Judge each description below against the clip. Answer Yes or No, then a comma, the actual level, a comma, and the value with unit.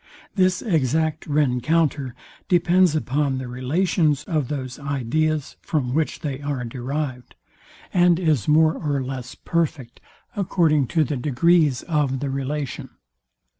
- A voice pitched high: No, medium, 150 Hz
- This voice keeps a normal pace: No, slow, 125 wpm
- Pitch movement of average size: Yes, average, 3.5 semitones